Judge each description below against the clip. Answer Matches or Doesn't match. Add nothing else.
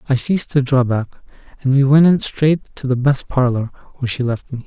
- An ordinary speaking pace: Doesn't match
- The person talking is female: Doesn't match